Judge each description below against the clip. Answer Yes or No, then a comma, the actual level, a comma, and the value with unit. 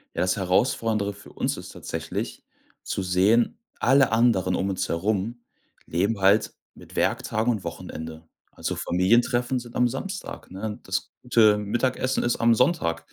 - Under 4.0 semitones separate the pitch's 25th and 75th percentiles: No, average, 4.3 semitones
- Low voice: Yes, low, 105 Hz